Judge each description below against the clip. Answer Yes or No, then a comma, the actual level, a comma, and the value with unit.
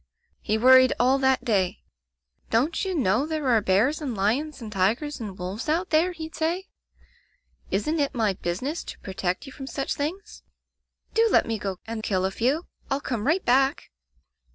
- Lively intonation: Yes, wide, 6.5 semitones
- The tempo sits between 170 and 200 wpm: Yes, average, 185 wpm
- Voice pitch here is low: No, very high, 260 Hz